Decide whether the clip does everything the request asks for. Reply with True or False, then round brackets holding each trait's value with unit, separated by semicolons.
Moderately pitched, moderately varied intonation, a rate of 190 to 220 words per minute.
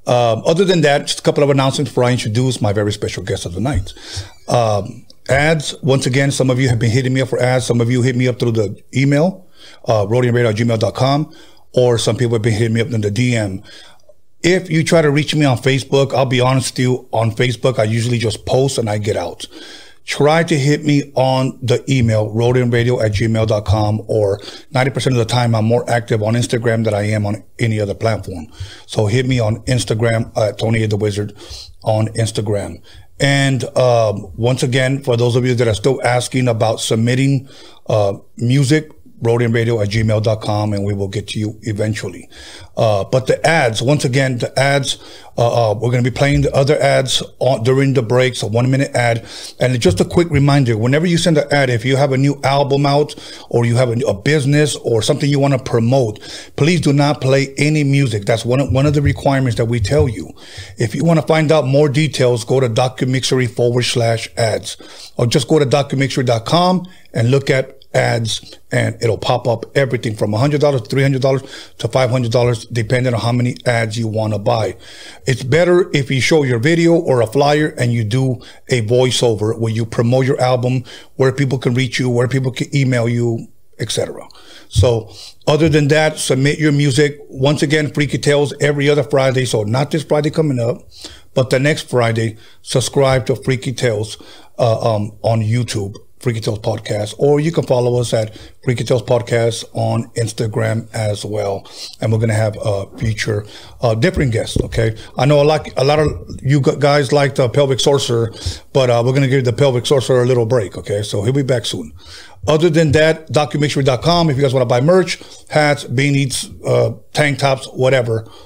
False (125 Hz; 3.6 semitones; 200 wpm)